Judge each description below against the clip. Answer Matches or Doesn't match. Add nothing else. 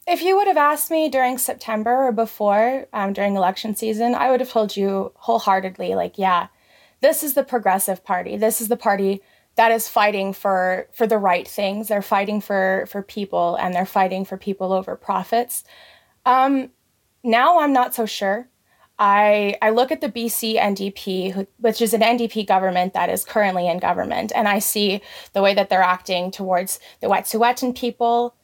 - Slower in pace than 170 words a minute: Doesn't match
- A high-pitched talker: Matches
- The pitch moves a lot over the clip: Doesn't match